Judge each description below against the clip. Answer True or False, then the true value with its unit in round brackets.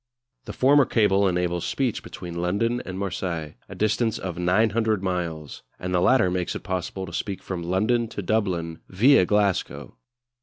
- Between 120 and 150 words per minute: False (160 wpm)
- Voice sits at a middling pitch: False (95 Hz)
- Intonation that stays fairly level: False (3.7 semitones)